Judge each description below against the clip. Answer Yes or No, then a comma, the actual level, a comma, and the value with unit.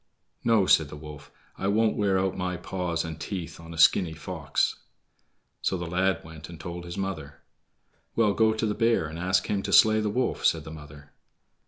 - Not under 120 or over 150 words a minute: No, average, 200 wpm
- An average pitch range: Yes, average, 3.9 semitones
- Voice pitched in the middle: No, very low, 90 Hz